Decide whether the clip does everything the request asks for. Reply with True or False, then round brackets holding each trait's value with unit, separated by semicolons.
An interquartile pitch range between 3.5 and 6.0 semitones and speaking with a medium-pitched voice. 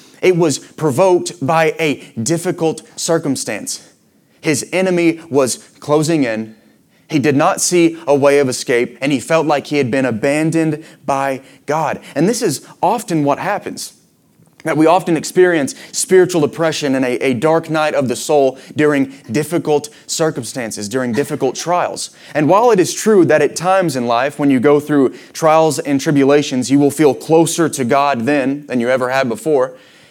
False (3.1 semitones; 150 Hz)